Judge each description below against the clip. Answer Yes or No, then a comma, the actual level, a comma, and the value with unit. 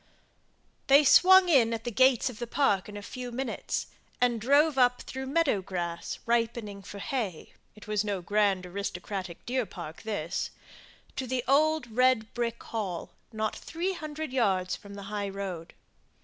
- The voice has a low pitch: No, high, 225 Hz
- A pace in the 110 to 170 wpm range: Yes, average, 165 wpm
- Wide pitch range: No, average, 4.7 semitones